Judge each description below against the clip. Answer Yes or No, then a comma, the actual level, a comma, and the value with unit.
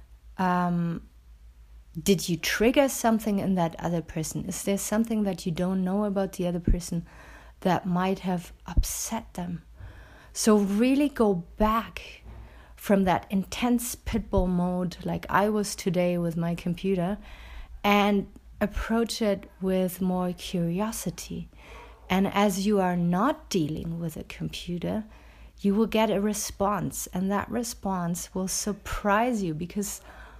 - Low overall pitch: No, high, 190 Hz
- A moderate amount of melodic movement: Yes, average, 3.0 semitones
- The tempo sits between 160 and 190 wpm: No, slow, 135 wpm